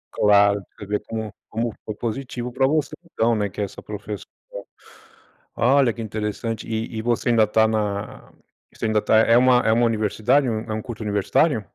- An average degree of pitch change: No, narrow, 2.1 semitones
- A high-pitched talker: No, low, 110 Hz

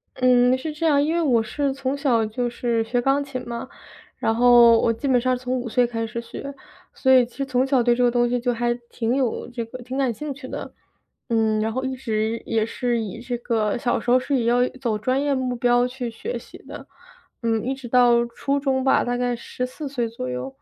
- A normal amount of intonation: No, narrow, 2.0 semitones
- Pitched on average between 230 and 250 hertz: Yes, high, 245 Hz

